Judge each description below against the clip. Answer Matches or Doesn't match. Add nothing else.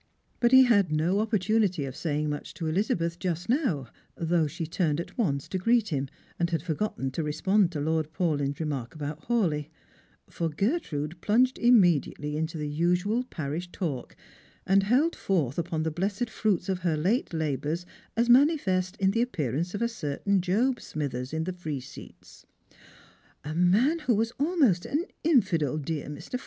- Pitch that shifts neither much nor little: Doesn't match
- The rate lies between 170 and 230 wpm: Matches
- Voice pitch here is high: Doesn't match